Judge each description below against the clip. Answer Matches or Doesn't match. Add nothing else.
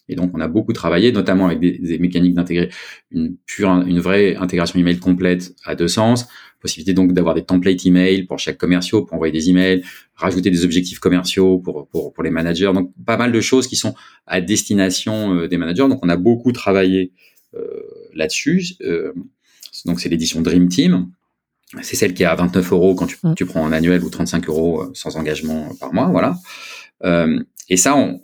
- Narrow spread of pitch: Matches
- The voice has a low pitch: Matches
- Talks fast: Doesn't match